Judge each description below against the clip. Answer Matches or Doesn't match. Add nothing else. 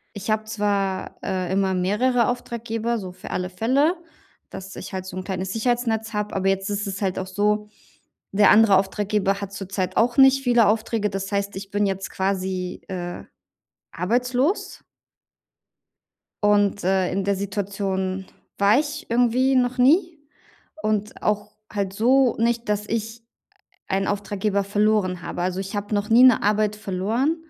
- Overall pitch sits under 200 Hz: Doesn't match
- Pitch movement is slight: Doesn't match